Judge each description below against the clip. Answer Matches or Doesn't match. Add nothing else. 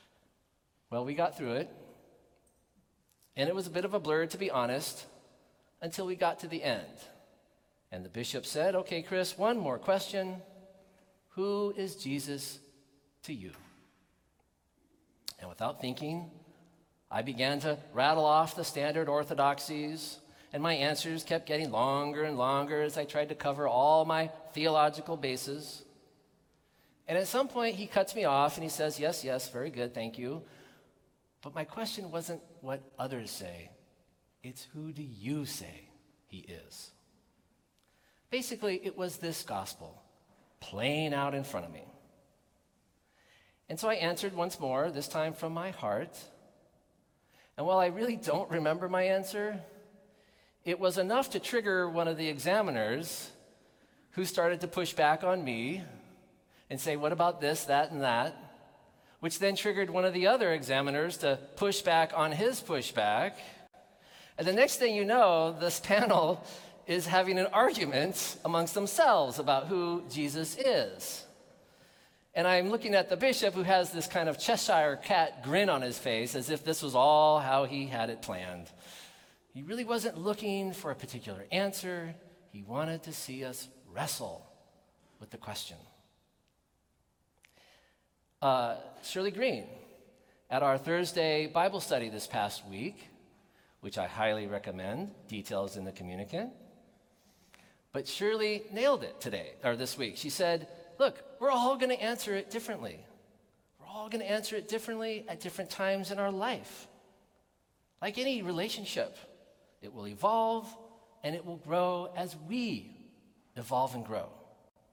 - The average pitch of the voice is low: Doesn't match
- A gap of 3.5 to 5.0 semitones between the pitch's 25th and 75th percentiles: Doesn't match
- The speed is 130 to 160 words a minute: Matches